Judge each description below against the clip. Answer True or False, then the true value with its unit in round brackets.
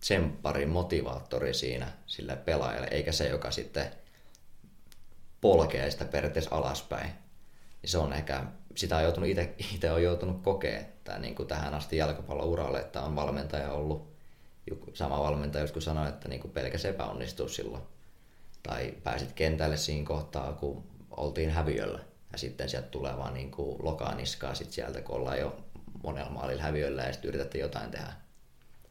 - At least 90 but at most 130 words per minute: False (140 wpm)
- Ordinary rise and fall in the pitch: False (2.3 semitones)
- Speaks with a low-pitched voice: True (75 Hz)